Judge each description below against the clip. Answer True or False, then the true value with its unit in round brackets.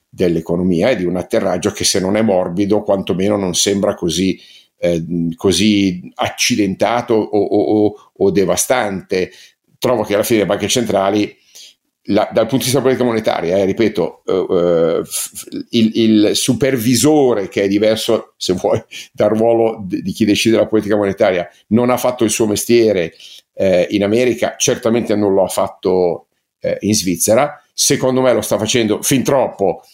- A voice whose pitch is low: True (105 Hz)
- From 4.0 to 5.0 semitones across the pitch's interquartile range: False (2.8 semitones)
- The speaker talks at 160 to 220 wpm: True (165 wpm)